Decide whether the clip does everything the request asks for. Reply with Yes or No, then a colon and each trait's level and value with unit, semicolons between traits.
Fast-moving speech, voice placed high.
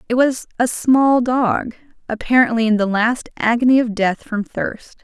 No: average, 165 wpm; high, 235 Hz